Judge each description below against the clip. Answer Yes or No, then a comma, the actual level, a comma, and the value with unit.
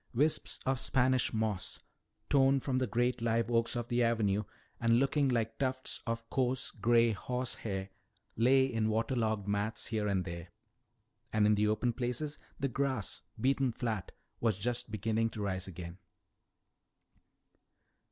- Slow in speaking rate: No, average, 145 wpm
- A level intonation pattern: No, average, 3.1 semitones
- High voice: No, low, 115 Hz